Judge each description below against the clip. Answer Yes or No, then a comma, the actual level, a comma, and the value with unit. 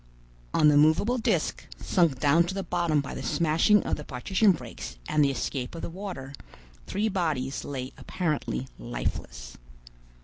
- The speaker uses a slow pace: No, average, 160 wpm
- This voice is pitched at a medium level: Yes, medium, 155 Hz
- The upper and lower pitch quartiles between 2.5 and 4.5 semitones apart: No, average, 5.3 semitones